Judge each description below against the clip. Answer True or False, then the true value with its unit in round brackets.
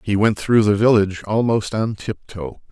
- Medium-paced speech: True (175 wpm)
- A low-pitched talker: True (100 Hz)